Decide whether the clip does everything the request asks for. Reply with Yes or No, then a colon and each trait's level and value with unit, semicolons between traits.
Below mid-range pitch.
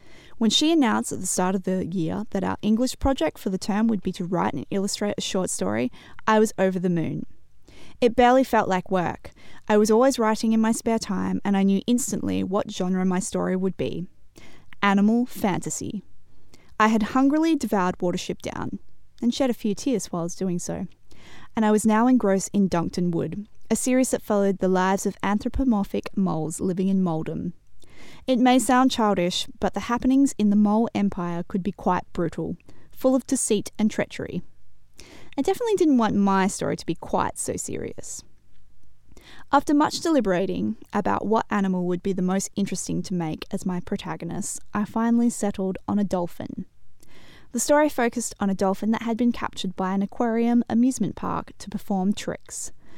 No: high, 205 Hz